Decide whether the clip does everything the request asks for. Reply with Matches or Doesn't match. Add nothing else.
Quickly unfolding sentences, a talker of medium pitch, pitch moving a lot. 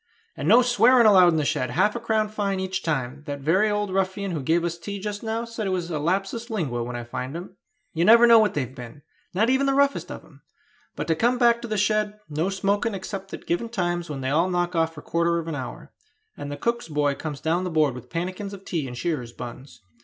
Matches